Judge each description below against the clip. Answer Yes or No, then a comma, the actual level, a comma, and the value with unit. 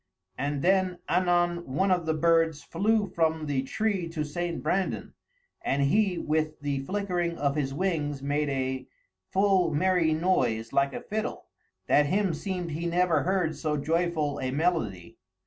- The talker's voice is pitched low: No, medium, 165 Hz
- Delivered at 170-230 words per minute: No, average, 155 wpm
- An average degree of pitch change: Yes, average, 3.8 semitones